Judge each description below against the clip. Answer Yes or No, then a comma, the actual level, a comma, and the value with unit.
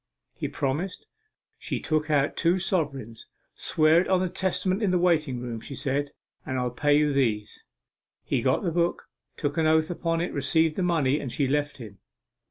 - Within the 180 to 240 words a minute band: Yes, average, 185 wpm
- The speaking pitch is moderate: Yes, medium, 150 Hz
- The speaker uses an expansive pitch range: No, average, 4.0 semitones